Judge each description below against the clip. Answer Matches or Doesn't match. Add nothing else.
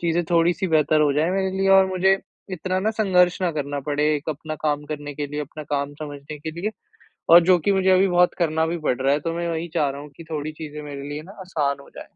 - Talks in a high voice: Doesn't match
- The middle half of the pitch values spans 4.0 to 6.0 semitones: Doesn't match